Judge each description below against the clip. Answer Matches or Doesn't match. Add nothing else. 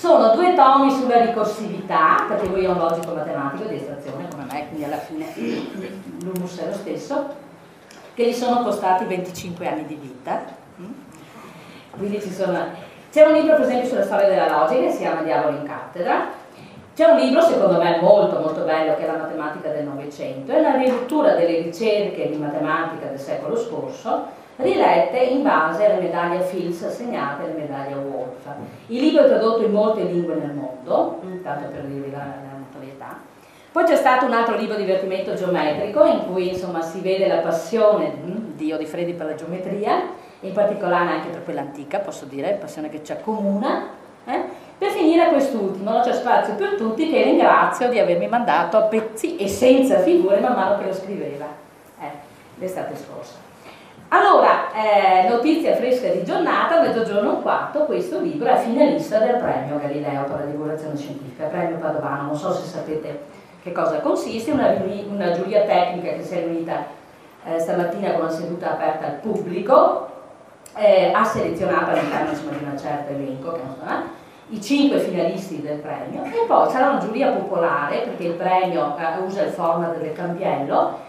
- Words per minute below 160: Doesn't match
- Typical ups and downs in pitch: Doesn't match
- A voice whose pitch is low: Doesn't match